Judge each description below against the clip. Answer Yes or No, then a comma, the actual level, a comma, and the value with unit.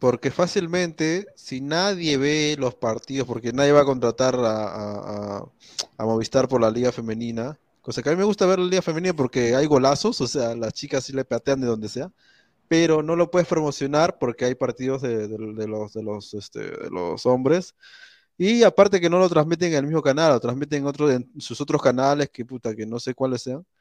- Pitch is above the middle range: No, low, 135 Hz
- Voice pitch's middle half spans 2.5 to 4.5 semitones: No, average, 5.3 semitones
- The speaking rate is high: Yes, fast, 220 wpm